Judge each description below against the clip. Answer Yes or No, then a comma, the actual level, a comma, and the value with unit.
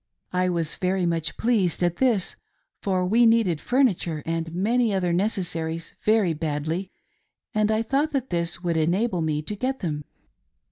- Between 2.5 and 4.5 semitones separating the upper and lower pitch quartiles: No, average, 4.9 semitones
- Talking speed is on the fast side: No, average, 155 wpm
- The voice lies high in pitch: No, medium, 180 Hz